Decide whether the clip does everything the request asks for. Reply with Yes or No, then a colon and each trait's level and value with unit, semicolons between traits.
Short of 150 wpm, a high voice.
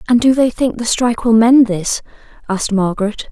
No: average, 200 wpm; high, 225 Hz